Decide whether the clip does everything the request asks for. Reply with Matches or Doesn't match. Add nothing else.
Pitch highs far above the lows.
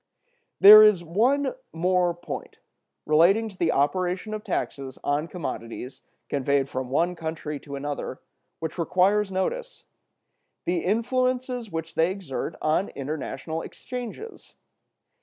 Matches